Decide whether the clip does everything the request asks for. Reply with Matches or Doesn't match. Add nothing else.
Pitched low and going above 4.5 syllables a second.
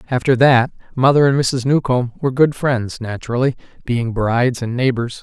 Matches